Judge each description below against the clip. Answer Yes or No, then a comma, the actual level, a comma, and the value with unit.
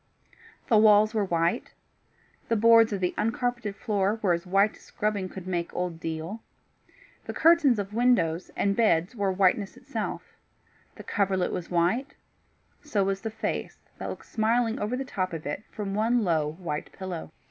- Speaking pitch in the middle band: No, high, 200 Hz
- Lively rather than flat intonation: No, average, 3.9 semitones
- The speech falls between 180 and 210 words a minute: No, average, 170 wpm